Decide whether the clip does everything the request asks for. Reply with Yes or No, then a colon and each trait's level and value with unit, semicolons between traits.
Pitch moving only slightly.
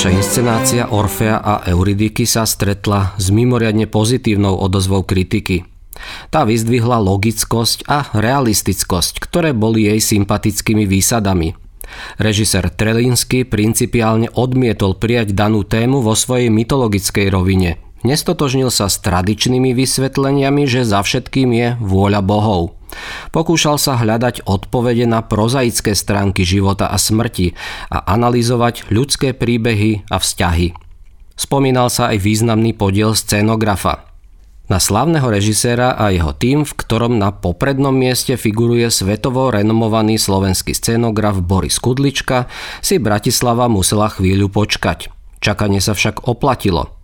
No: average, 3.5 semitones